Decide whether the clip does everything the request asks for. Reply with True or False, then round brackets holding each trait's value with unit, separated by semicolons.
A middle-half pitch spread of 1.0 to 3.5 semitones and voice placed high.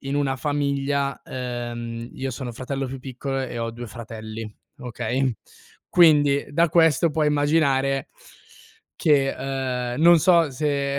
False (2.8 semitones; 135 Hz)